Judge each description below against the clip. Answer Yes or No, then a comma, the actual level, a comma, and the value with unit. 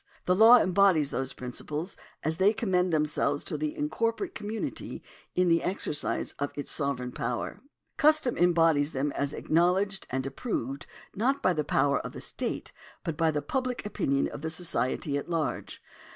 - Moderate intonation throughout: No, wide, 6.1 semitones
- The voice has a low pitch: No, medium, 165 Hz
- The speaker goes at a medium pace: Yes, average, 165 wpm